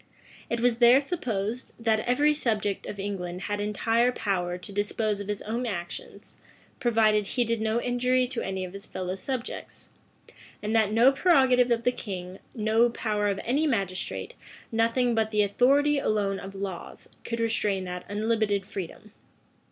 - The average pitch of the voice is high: Yes, high, 220 Hz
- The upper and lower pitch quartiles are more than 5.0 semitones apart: No, average, 3.4 semitones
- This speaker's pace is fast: No, average, 160 wpm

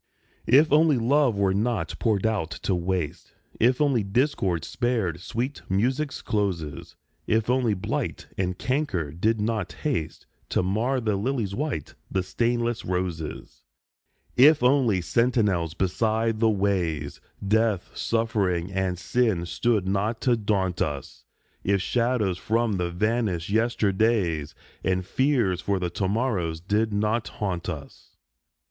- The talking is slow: Yes, slow, 130 wpm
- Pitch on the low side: Yes, low, 105 Hz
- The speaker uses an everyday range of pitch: Yes, average, 4.5 semitones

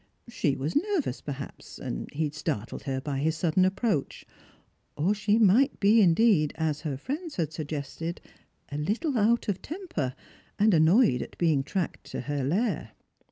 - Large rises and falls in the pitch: Yes, wide, 6.9 semitones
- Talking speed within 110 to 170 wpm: Yes, average, 160 wpm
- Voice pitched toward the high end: No, medium, 165 Hz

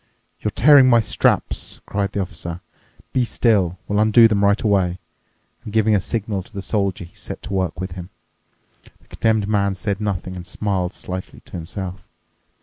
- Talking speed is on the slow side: No, average, 175 wpm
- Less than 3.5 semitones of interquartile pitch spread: Yes, average, 2.7 semitones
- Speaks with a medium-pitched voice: No, low, 100 Hz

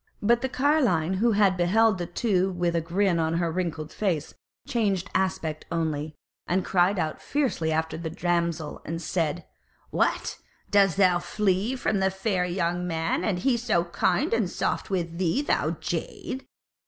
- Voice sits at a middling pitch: Yes, medium, 180 Hz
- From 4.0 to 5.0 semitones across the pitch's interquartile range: No, average, 3.3 semitones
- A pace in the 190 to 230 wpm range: No, average, 165 wpm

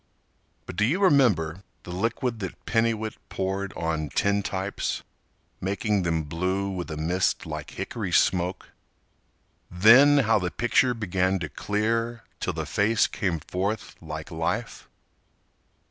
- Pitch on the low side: Yes, very low, 95 Hz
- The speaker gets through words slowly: Yes, slow, 130 wpm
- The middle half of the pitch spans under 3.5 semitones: No, average, 4.1 semitones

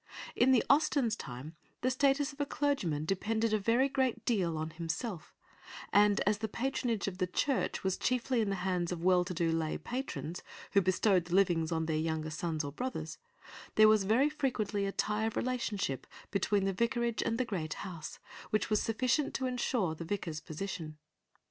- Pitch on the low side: No, high, 200 Hz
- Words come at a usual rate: Yes, average, 190 wpm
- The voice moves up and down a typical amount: No, wide, 6.1 semitones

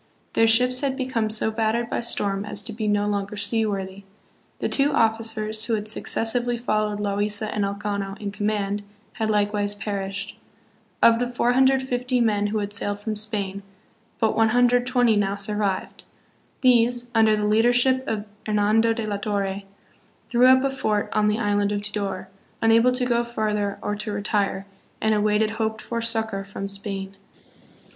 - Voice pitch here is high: Yes, high, 215 Hz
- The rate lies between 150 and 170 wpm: Yes, average, 160 wpm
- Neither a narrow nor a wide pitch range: No, narrow, 2.3 semitones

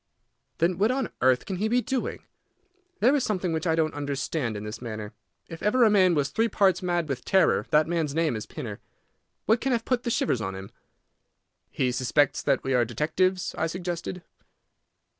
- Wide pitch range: Yes, wide, 7.0 semitones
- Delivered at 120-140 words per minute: No, average, 195 wpm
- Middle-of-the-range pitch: Yes, medium, 165 Hz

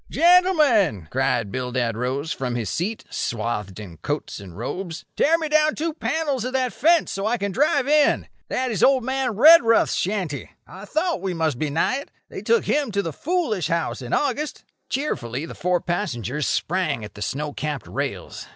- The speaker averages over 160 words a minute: Yes, average, 185 wpm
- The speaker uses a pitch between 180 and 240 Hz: Yes, high, 190 Hz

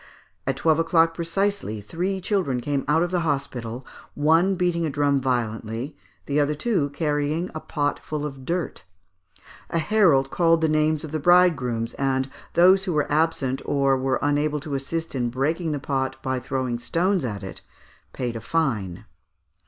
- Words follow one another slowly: No, average, 170 wpm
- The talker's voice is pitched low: No, medium, 145 Hz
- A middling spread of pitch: Yes, average, 3.9 semitones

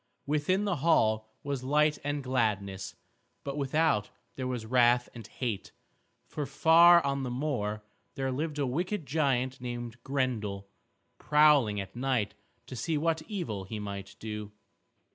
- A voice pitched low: Yes, low, 130 Hz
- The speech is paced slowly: No, average, 145 wpm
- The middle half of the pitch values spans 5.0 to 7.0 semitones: Yes, wide, 5.4 semitones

